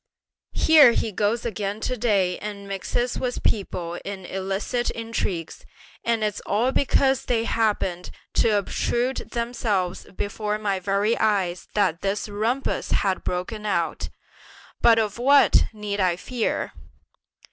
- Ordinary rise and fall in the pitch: Yes, average, 3.2 semitones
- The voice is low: No, high, 210 Hz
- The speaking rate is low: Yes, slow, 130 wpm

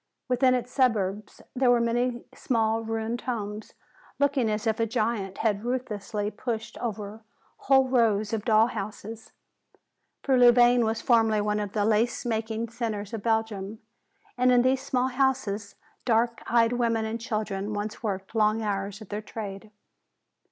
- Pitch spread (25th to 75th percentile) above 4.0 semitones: No, narrow, 2.4 semitones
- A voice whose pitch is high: Yes, high, 225 Hz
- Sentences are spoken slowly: No, average, 150 wpm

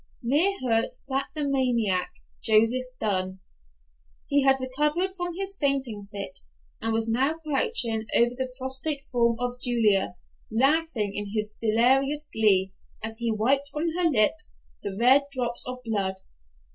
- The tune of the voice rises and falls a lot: No, average, 4.3 semitones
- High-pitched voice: Yes, very high, 250 Hz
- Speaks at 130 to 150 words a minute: Yes, average, 140 wpm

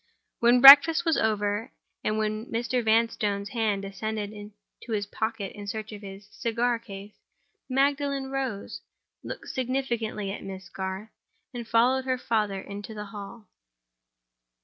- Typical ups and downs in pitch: Yes, average, 3.1 semitones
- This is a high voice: Yes, high, 220 Hz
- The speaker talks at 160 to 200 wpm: No, slow, 135 wpm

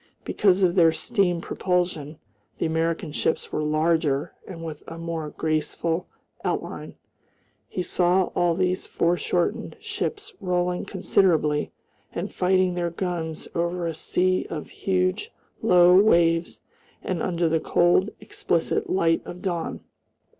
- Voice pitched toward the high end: No, medium, 175 Hz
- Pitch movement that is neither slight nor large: No, narrow, 2.0 semitones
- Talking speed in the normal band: No, slow, 125 wpm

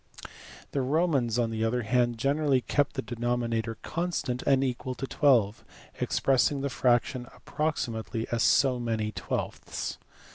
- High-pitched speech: No, low, 125 Hz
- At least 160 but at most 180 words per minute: No, average, 140 wpm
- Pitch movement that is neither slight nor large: Yes, average, 3.0 semitones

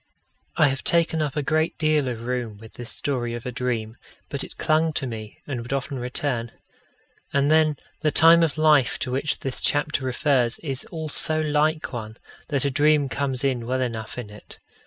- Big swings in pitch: No, average, 3.9 semitones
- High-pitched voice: No, low, 135 Hz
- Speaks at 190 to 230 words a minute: Yes, average, 200 wpm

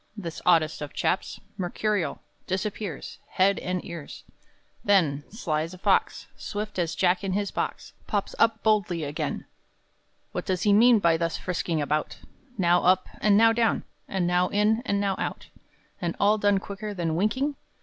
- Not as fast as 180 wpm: Yes, average, 165 wpm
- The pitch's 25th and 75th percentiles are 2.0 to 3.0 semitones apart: No, average, 3.4 semitones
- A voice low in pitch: No, high, 190 Hz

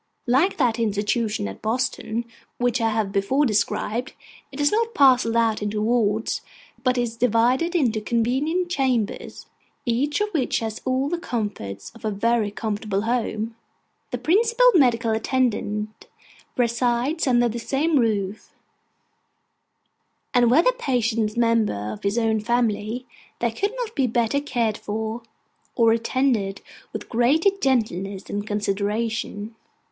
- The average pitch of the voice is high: Yes, high, 235 Hz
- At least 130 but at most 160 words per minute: Yes, slow, 135 wpm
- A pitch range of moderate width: Yes, average, 3.2 semitones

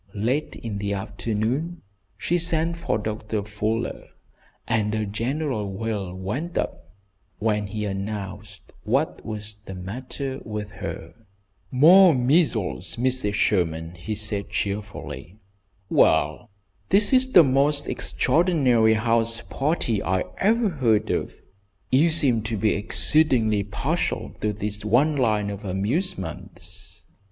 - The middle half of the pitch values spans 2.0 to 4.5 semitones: No, average, 5.1 semitones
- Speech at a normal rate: No, slow, 120 wpm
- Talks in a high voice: No, low, 110 Hz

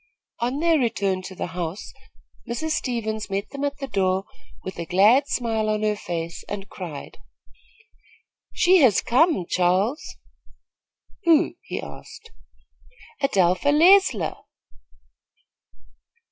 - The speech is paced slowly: Yes, slow, 115 wpm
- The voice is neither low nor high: No, high, 215 Hz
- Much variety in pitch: Yes, wide, 7.2 semitones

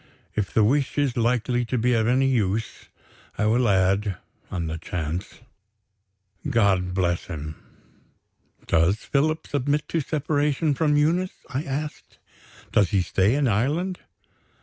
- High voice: No, low, 120 Hz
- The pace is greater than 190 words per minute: No, slow, 135 wpm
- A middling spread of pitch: No, wide, 7.0 semitones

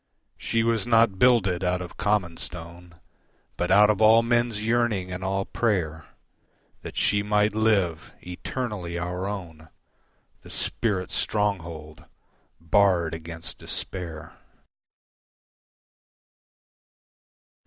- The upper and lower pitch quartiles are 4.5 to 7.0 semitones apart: No, average, 3.9 semitones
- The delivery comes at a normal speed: No, slow, 100 wpm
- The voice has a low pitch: Yes, very low, 95 Hz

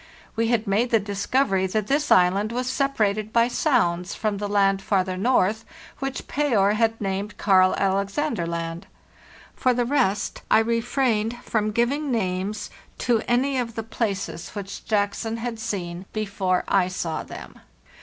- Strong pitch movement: No, average, 3.5 semitones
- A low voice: No, high, 215 Hz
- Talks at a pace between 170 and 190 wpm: No, average, 155 wpm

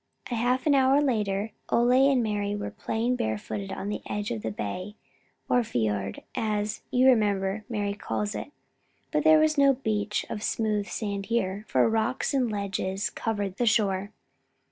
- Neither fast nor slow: Yes, average, 165 wpm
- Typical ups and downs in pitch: Yes, average, 3.6 semitones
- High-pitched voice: Yes, high, 210 Hz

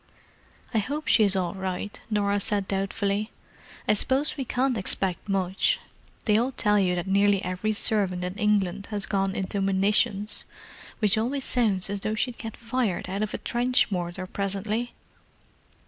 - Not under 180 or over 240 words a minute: No, average, 155 wpm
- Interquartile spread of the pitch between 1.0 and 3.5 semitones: Yes, narrow, 2.5 semitones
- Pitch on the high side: Yes, high, 205 Hz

